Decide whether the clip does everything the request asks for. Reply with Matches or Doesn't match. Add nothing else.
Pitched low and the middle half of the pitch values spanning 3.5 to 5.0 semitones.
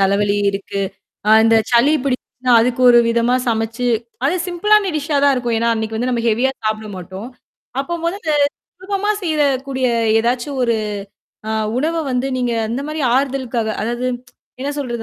Doesn't match